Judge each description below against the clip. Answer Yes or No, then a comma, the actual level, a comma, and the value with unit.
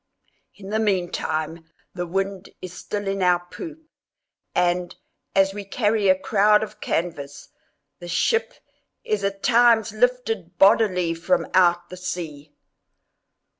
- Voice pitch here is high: Yes, high, 195 Hz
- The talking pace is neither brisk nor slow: No, slow, 130 wpm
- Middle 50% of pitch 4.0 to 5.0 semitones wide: No, average, 3.3 semitones